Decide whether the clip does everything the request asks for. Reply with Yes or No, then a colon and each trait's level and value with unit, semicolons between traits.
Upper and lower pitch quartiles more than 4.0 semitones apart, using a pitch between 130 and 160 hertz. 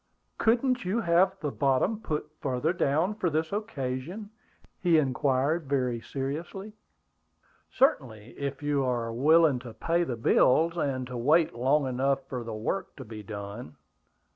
Yes: average, 5.2 semitones; medium, 140 Hz